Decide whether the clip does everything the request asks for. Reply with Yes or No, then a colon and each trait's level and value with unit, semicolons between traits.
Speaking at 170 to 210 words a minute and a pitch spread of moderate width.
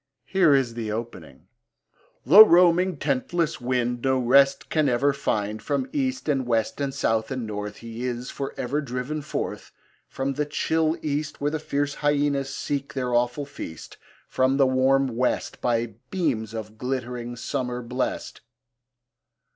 No: average, 145 wpm; average, 3.3 semitones